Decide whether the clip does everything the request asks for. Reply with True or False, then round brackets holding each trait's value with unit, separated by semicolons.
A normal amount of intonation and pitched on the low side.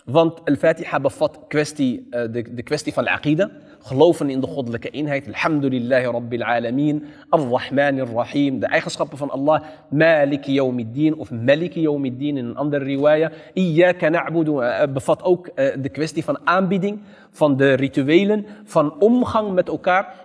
False (3.3 semitones; 150 Hz)